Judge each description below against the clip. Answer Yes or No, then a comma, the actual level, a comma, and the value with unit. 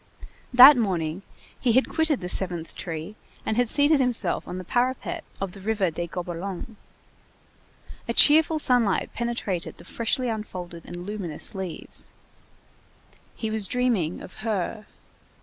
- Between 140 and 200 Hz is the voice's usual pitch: No, high, 215 Hz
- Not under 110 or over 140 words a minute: Yes, slow, 135 wpm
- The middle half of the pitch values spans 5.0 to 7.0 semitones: Yes, wide, 5.6 semitones